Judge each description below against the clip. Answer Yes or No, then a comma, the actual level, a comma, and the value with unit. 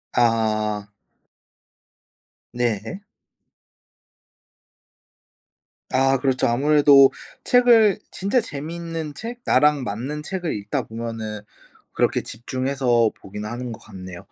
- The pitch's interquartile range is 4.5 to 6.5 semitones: Yes, average, 5.2 semitones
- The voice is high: No, low, 130 Hz